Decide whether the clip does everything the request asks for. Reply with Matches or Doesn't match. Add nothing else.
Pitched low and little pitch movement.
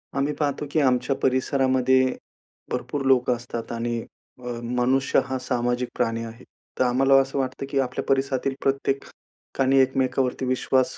Matches